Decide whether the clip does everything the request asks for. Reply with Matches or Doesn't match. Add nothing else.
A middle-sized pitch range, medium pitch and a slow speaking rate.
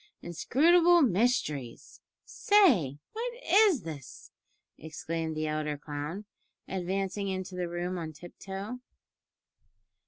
Doesn't match